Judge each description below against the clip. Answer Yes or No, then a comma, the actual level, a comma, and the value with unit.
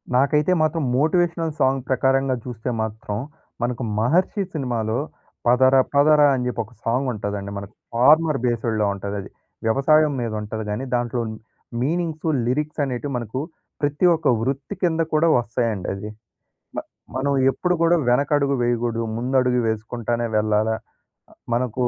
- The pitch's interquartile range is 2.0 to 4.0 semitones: No, average, 4.4 semitones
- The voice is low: Yes, low, 125 Hz